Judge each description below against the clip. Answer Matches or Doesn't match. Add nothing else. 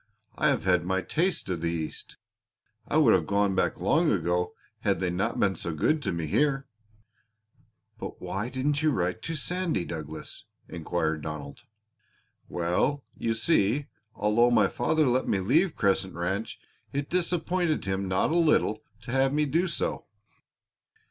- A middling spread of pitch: Doesn't match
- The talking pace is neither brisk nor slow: Matches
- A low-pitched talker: Matches